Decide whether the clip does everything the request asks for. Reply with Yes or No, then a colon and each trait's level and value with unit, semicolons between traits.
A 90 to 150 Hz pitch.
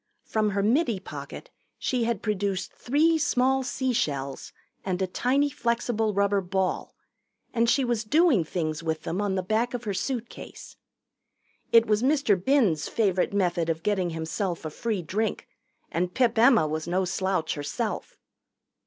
No: high, 205 Hz